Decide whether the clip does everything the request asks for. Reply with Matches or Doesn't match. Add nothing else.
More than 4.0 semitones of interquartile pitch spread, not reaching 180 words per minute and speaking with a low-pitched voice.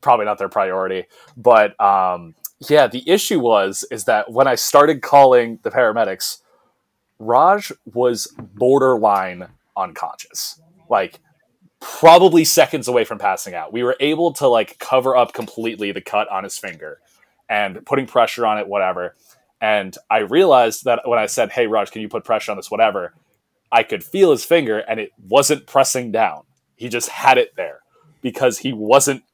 Matches